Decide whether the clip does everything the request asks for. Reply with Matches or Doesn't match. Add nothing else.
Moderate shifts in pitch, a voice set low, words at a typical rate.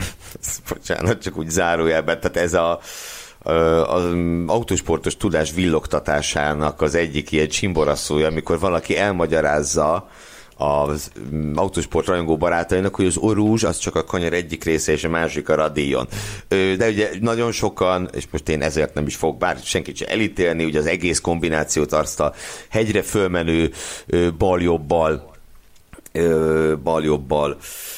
Matches